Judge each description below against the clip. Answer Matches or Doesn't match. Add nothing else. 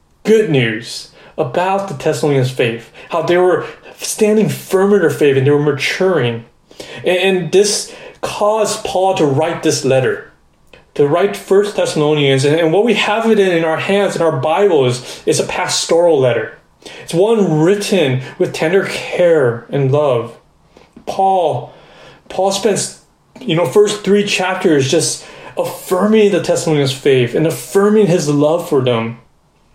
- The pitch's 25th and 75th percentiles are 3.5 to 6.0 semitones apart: Matches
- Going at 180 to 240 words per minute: Doesn't match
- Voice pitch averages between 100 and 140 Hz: Doesn't match